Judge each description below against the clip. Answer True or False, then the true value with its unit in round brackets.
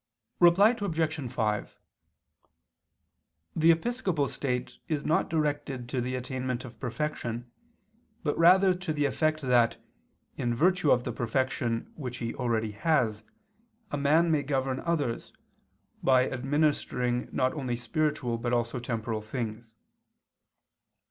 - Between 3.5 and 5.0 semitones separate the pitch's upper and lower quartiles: True (4.5 semitones)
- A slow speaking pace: True (120 wpm)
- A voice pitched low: True (130 Hz)